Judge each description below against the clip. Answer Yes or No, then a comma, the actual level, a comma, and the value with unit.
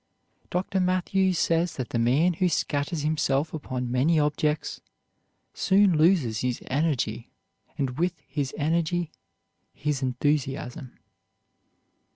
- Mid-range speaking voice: Yes, medium, 150 Hz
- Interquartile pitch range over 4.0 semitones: Yes, average, 4.4 semitones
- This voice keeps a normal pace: No, slow, 110 wpm